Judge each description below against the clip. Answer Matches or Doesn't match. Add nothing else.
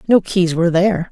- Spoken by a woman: Matches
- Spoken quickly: Matches